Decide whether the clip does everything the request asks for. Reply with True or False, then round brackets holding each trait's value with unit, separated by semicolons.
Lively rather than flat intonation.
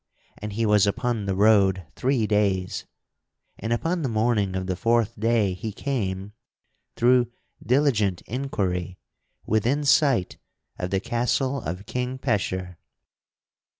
False (4.4 semitones)